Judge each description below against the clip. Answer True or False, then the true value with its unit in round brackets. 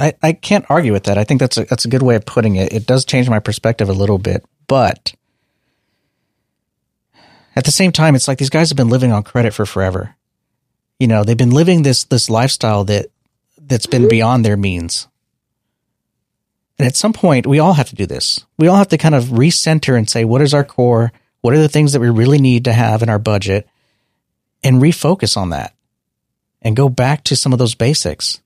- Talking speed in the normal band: False (215 wpm)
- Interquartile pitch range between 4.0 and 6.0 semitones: True (4.7 semitones)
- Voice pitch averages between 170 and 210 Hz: False (125 Hz)